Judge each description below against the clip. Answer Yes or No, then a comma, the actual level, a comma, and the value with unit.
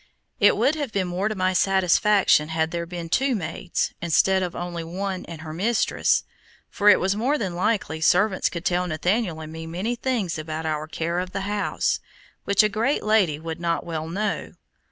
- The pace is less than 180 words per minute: No, average, 195 wpm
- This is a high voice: No, medium, 180 Hz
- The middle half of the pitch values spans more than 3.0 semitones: Yes, average, 3.9 semitones